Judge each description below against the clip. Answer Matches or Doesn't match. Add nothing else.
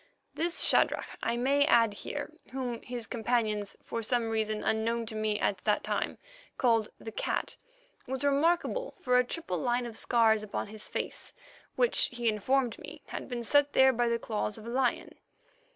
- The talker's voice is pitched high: Matches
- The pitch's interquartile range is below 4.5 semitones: Matches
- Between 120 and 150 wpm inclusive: Doesn't match